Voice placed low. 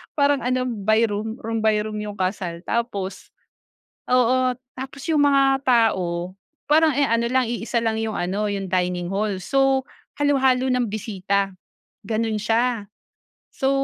No: high, 225 Hz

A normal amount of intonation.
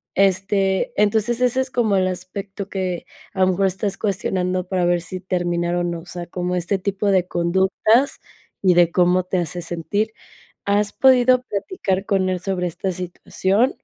No: narrow, 2.1 semitones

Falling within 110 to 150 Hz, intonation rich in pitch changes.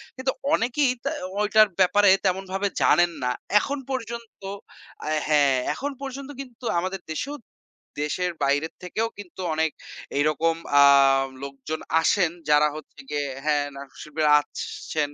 No: medium, 180 Hz; wide, 7.1 semitones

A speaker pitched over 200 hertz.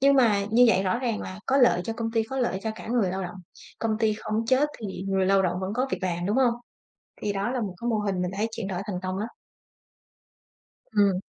Yes: high, 210 Hz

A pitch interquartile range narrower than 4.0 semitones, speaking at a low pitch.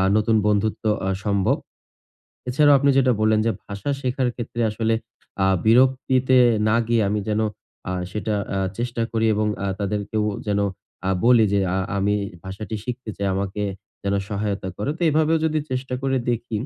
Yes: average, 3.6 semitones; low, 110 Hz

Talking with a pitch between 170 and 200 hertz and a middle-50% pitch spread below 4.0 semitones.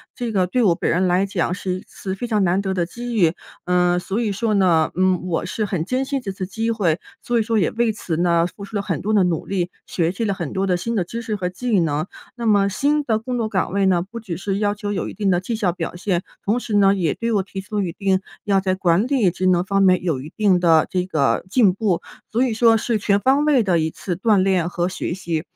Yes: high, 195 Hz; average, 3.4 semitones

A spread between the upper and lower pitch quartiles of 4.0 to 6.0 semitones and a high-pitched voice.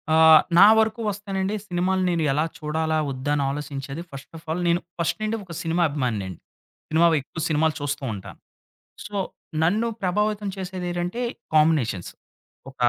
No: average, 4.6 semitones; medium, 165 Hz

